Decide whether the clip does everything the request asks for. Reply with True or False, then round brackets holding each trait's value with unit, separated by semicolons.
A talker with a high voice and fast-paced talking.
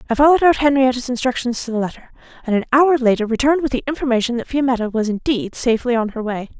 True (250 Hz; 220 wpm)